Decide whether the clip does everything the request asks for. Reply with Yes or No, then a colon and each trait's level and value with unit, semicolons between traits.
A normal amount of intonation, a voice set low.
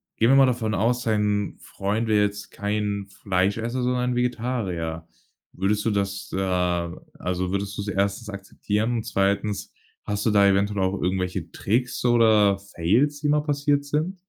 Yes: average, 3.5 semitones; low, 105 Hz